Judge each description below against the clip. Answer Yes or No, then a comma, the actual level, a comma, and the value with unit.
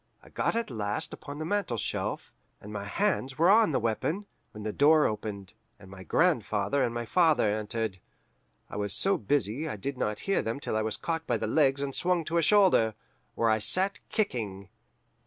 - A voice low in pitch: Yes, low, 120 Hz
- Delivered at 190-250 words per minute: Yes, average, 195 wpm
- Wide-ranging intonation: Yes, wide, 7.3 semitones